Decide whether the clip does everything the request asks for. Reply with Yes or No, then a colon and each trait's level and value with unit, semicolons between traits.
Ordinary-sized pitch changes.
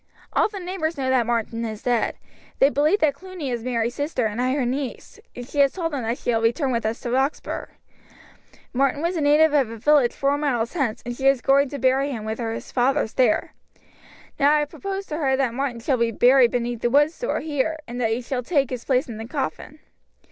Yes: average, 3.5 semitones